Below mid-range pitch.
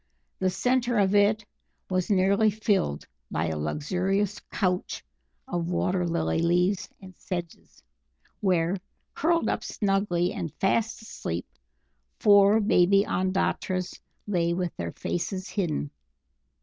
No: medium, 185 Hz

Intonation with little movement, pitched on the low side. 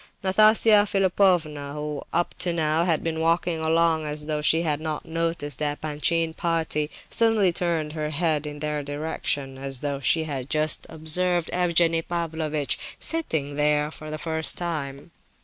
No: narrow, 2.2 semitones; medium, 160 Hz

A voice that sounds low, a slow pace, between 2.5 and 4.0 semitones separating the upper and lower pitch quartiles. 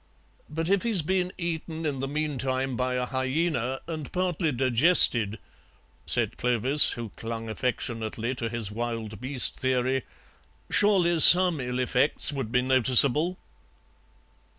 No: low, 130 Hz; slow, 125 wpm; average, 4.8 semitones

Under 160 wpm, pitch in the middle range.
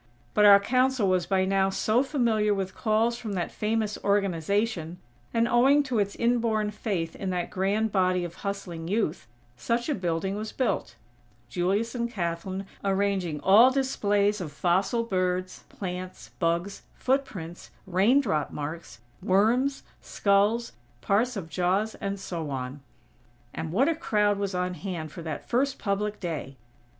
No: average, 145 wpm; high, 200 Hz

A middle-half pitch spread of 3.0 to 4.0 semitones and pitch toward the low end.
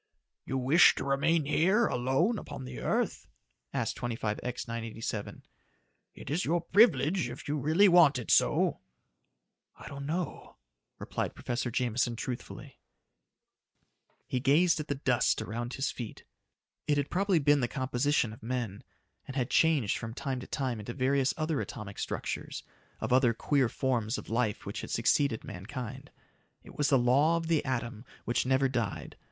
Yes: average, 3.7 semitones; low, 130 Hz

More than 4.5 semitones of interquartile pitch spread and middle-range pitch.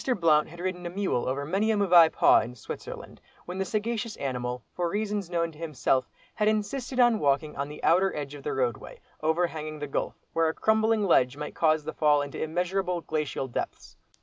Yes: average, 5.0 semitones; medium, 165 Hz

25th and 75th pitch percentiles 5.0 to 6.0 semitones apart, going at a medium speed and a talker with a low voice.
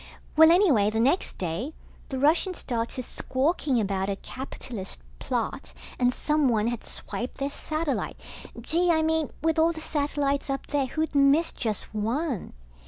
No: wide, 5.4 semitones; average, 150 wpm; very high, 275 Hz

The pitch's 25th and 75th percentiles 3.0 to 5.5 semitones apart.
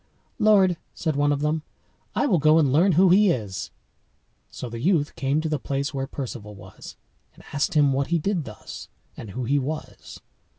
Yes: average, 4.0 semitones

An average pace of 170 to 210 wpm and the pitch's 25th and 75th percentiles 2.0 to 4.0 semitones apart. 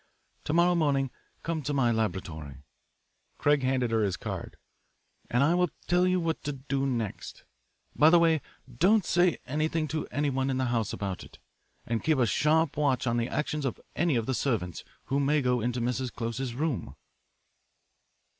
No: average, 175 wpm; average, 4.7 semitones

